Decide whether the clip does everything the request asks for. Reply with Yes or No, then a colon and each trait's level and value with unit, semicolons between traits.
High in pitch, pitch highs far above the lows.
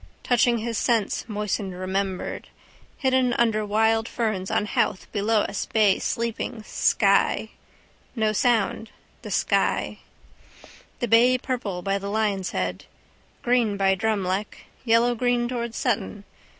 No: high, 220 Hz; average, 3.0 semitones